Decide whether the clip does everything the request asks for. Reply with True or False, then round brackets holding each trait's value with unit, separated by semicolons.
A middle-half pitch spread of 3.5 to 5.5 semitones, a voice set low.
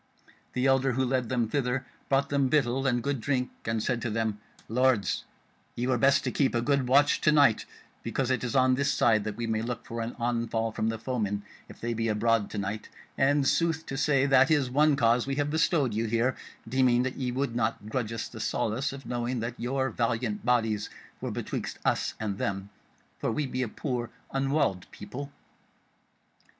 False (3.1 semitones; 125 Hz)